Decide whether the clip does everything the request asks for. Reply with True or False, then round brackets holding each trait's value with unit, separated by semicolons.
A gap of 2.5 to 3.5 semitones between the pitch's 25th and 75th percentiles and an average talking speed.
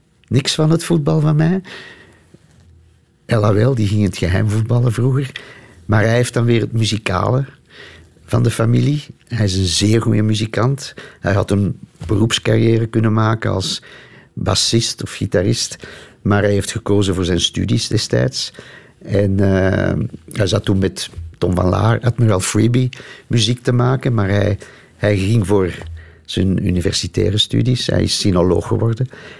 False (3.9 semitones; 150 wpm)